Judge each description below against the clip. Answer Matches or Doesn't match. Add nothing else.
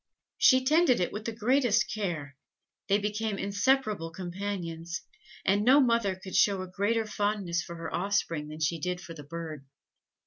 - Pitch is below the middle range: Doesn't match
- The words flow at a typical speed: Matches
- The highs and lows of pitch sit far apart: Doesn't match